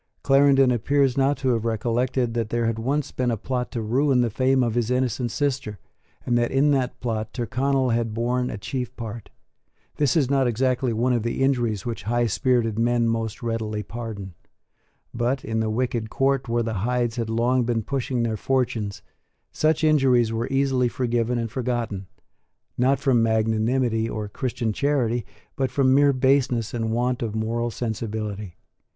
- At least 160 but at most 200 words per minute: Yes, average, 170 wpm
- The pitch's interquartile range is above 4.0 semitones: No, narrow, 2.4 semitones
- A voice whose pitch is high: No, low, 120 Hz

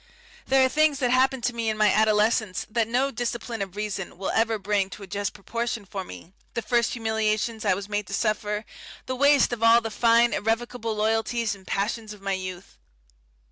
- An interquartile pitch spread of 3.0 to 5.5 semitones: No, narrow, 2.6 semitones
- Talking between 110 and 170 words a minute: No, average, 200 wpm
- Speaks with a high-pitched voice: Yes, high, 220 Hz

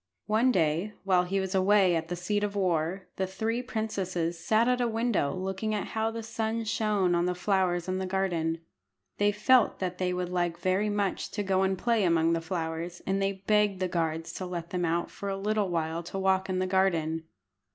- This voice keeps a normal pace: No, fast, 215 wpm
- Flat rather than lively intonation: No, average, 3.1 semitones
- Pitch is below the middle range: No, high, 190 Hz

